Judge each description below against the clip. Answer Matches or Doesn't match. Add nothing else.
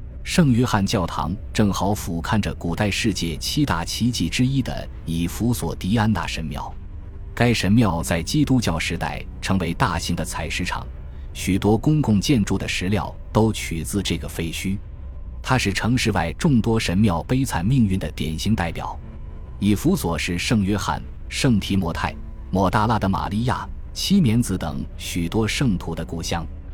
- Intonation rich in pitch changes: Doesn't match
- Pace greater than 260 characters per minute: Doesn't match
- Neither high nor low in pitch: Doesn't match